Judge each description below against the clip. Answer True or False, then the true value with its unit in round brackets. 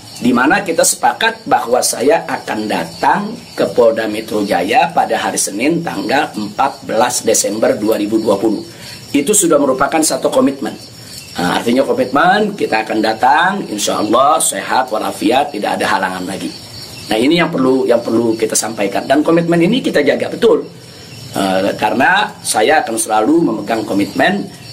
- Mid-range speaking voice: True (145 Hz)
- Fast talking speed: True (145 wpm)